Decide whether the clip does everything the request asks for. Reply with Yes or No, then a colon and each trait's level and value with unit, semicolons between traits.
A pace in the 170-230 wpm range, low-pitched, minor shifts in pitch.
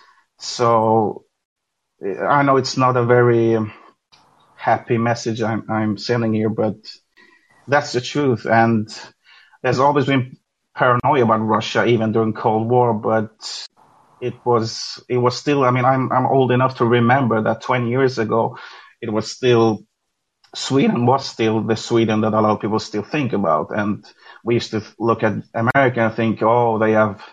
No: average, 160 wpm; low, 115 Hz; narrow, 2.1 semitones